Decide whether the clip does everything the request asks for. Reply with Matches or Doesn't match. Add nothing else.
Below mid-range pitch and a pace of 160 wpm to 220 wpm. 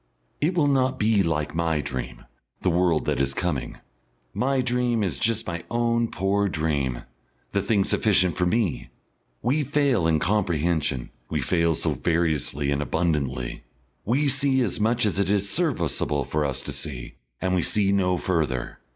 Matches